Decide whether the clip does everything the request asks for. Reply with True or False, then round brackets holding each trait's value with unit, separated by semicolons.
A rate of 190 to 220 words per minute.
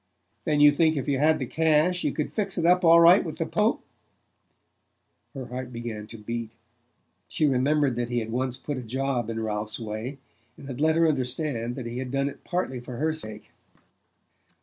True (200 wpm)